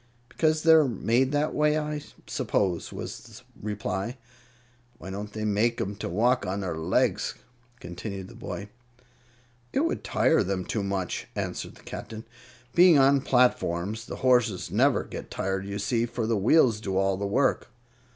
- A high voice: No, low, 110 Hz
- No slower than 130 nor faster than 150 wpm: No, average, 160 wpm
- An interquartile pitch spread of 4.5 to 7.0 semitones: Yes, average, 5.0 semitones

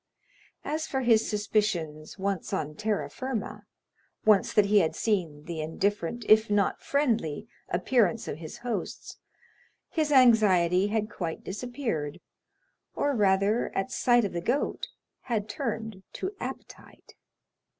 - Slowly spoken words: Yes, slow, 130 wpm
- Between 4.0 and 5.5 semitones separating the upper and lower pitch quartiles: Yes, average, 5.0 semitones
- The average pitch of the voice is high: Yes, high, 210 Hz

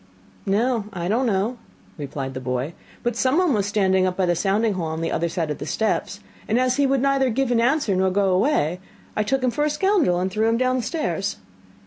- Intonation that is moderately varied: No, wide, 5.8 semitones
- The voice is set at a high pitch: Yes, high, 215 Hz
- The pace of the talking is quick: Yes, fast, 215 wpm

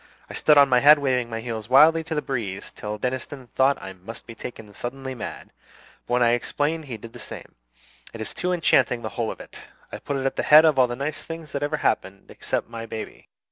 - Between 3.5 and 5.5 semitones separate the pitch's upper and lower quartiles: Yes, average, 4.2 semitones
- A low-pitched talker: Yes, low, 130 Hz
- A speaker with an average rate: No, fast, 240 wpm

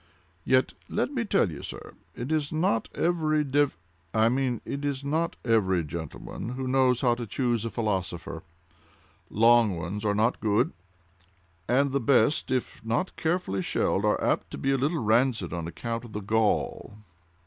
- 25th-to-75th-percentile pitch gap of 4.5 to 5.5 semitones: Yes, average, 5.0 semitones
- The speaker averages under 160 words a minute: No, average, 165 wpm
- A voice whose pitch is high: No, low, 120 Hz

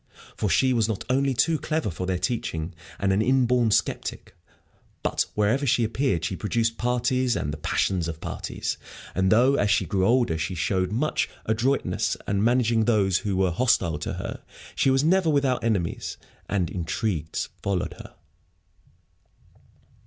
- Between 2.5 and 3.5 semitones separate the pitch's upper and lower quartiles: No, average, 5.3 semitones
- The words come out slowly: No, average, 160 wpm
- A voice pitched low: Yes, low, 110 Hz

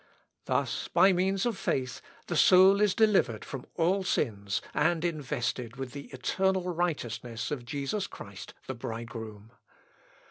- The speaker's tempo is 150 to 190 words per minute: No, slow, 135 wpm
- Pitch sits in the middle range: Yes, medium, 145 Hz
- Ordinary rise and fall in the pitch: No, wide, 7.8 semitones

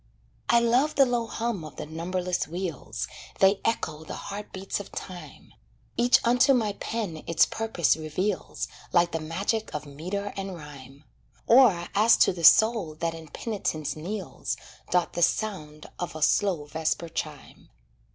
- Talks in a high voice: No, medium, 180 Hz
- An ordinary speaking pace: Yes, average, 155 wpm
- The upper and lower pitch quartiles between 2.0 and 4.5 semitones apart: No, wide, 5.4 semitones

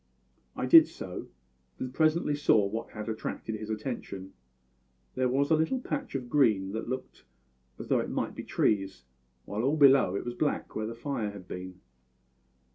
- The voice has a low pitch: Yes, low, 115 Hz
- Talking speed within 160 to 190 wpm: Yes, average, 175 wpm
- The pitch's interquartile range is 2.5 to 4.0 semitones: No, wide, 5.4 semitones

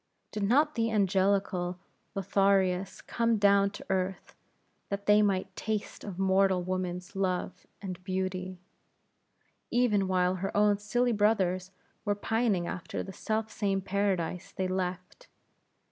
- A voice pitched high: Yes, high, 195 Hz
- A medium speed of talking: No, slow, 130 wpm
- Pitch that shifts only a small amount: Yes, narrow, 1.9 semitones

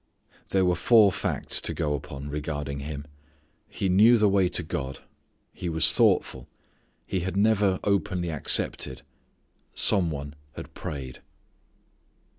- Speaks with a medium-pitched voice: No, very low, 85 Hz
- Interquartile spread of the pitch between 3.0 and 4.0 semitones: No, average, 5.1 semitones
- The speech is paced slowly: Yes, slow, 130 wpm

